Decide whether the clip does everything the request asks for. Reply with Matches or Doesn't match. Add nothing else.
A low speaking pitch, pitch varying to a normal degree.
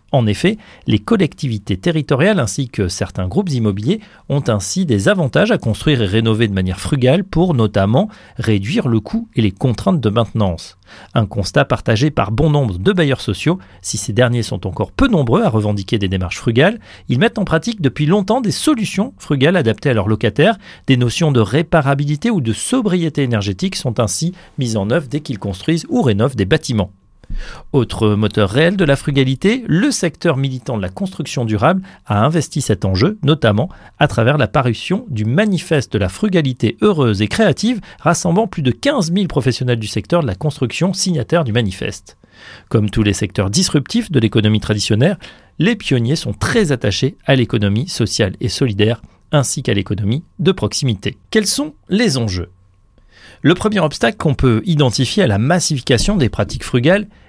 Doesn't match